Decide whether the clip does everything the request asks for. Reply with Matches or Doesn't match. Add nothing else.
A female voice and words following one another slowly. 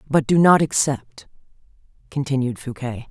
Matches